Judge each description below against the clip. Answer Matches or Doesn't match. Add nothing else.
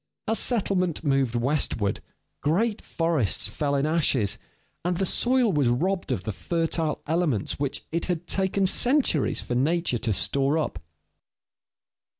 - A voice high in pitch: Doesn't match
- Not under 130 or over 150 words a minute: Matches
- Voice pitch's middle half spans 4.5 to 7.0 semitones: Matches